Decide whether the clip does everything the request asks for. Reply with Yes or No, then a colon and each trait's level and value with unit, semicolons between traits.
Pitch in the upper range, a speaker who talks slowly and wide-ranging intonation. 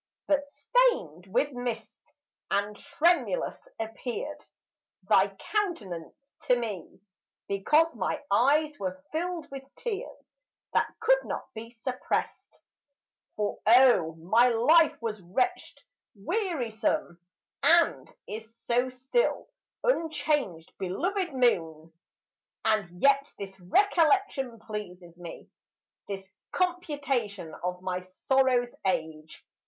Yes: high, 245 Hz; slow, 100 wpm; wide, 8.2 semitones